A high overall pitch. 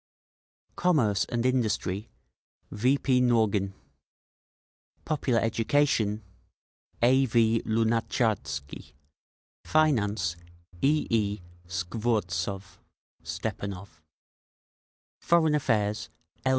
No: low, 110 Hz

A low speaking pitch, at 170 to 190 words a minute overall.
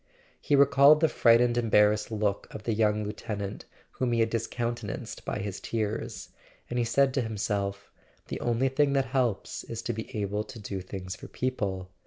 Yes: low, 115 Hz; average, 185 wpm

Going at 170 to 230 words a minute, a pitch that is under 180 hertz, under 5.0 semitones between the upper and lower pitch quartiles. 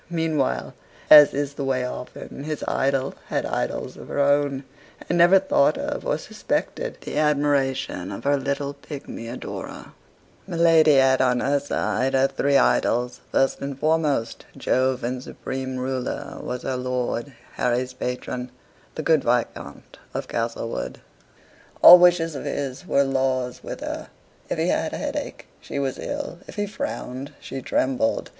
No: average, 155 wpm; low, 135 Hz; narrow, 2.4 semitones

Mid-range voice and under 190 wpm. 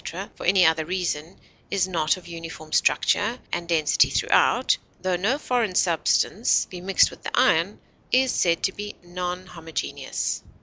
Yes: medium, 180 Hz; average, 160 wpm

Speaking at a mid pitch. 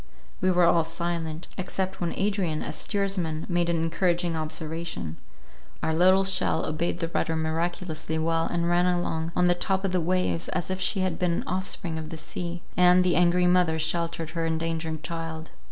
Yes: medium, 170 Hz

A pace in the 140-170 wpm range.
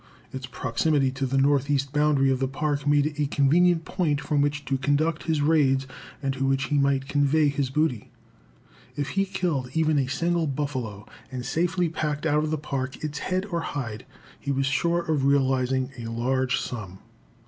No: average, 185 wpm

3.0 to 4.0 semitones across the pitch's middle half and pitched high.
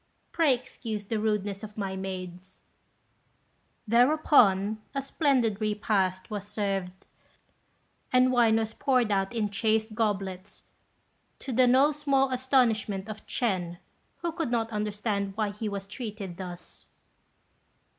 Yes: average, 3.7 semitones; high, 215 Hz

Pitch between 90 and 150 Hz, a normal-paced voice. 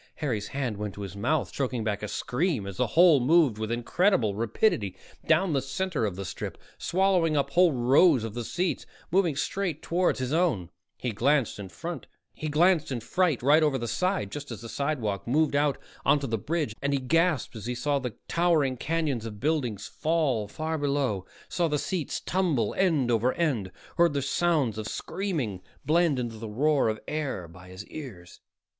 Yes: medium, 140 Hz; average, 180 wpm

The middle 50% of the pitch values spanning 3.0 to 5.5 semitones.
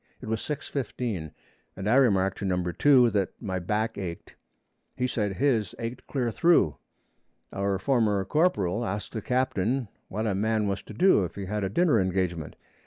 Yes: average, 4.5 semitones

